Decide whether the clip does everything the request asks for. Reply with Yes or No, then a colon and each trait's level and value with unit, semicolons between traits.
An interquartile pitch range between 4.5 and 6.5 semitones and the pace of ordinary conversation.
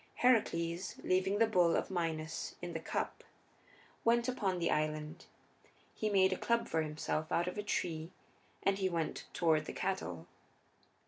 No: average, 3.5 semitones; average, 155 wpm